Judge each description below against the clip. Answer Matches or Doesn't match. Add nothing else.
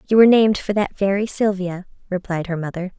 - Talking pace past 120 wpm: Matches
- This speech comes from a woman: Matches